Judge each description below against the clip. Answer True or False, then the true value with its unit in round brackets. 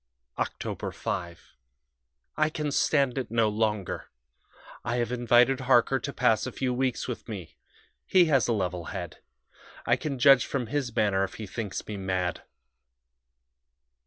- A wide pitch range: False (4.8 semitones)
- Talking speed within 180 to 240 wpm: False (150 wpm)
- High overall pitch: False (120 Hz)